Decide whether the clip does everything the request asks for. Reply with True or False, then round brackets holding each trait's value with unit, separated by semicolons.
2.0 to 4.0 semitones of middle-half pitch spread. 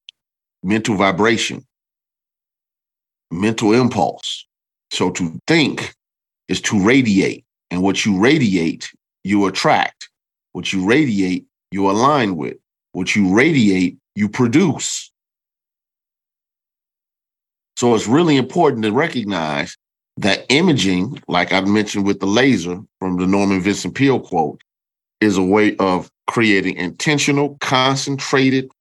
True (3.7 semitones)